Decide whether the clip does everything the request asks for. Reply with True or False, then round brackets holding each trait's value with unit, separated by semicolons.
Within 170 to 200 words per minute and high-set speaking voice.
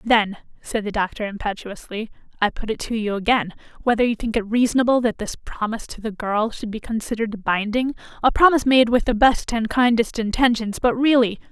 True (195 wpm; 225 Hz)